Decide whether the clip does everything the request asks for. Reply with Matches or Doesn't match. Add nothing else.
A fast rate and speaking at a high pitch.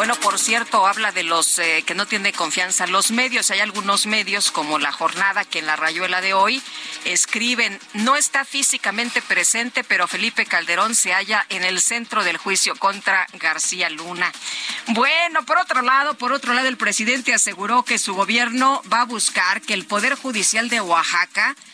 Doesn't match